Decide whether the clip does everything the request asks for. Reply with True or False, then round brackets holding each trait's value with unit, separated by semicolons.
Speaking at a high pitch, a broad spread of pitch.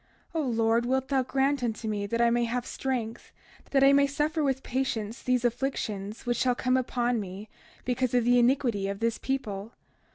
False (245 Hz; 2.8 semitones)